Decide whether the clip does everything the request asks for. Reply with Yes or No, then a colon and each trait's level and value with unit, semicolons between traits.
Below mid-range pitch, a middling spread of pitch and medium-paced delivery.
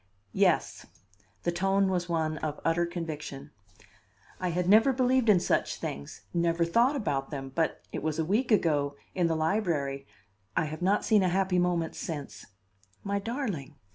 No: medium, 170 Hz; average, 4.1 semitones; average, 170 wpm